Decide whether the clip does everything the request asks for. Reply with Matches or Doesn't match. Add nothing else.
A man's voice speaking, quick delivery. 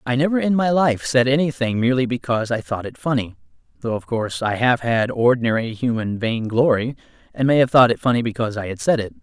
Matches